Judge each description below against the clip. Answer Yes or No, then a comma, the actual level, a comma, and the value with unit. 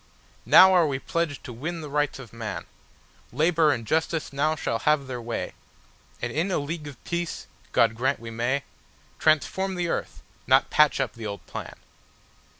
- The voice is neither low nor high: Yes, medium, 145 Hz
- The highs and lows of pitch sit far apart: No, average, 4.8 semitones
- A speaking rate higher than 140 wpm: Yes, average, 155 wpm